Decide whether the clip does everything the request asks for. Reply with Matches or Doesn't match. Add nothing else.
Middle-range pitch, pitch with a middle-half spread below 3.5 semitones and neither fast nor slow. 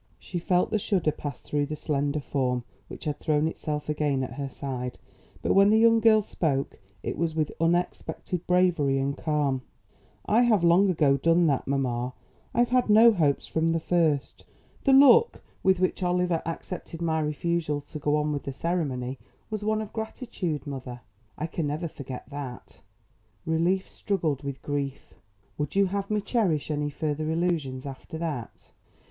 Doesn't match